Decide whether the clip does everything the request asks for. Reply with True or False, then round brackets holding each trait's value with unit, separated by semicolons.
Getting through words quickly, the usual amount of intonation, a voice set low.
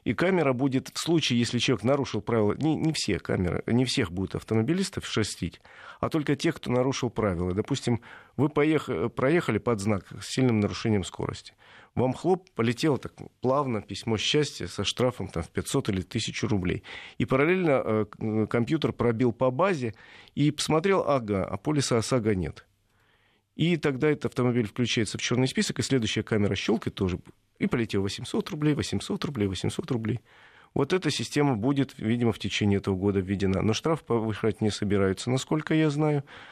True (170 wpm; 5.0 semitones; 120 Hz)